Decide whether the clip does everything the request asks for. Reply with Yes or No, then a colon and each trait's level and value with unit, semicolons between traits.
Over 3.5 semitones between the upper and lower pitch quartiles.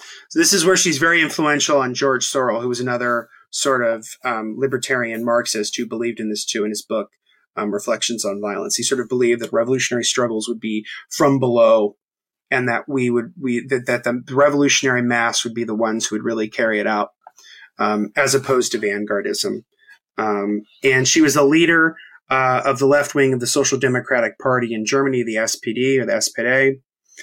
No: average, 3.0 semitones